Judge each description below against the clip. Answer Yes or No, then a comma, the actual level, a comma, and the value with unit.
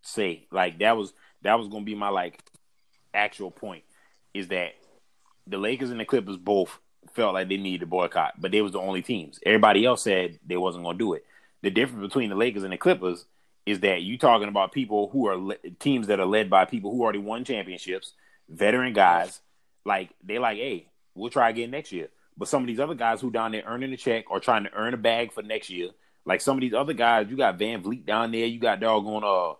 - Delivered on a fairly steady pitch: No, average, 3.5 semitones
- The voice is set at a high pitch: No, low, 110 Hz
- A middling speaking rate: No, fast, 235 wpm